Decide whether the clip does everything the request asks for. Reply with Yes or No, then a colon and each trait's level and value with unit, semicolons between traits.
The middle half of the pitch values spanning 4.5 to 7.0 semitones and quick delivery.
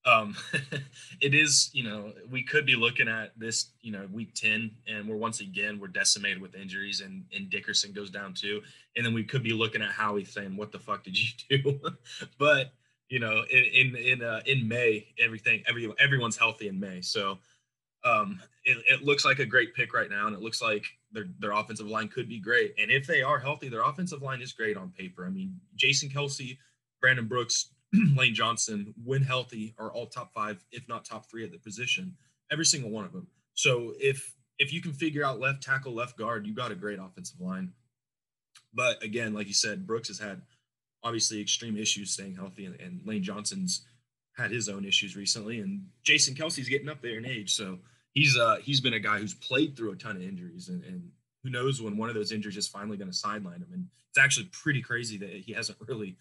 Yes: average, 5.1 semitones; fast, 215 wpm